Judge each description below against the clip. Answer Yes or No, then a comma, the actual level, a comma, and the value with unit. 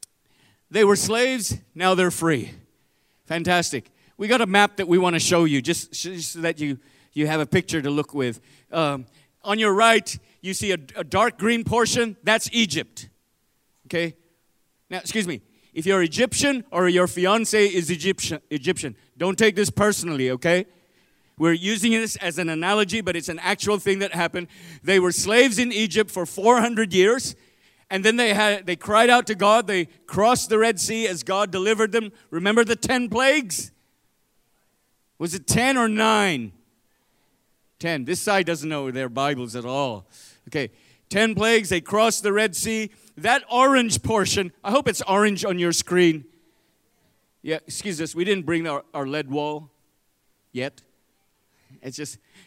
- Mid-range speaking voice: Yes, medium, 180 Hz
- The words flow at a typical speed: Yes, average, 170 wpm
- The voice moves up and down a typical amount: No, wide, 5.7 semitones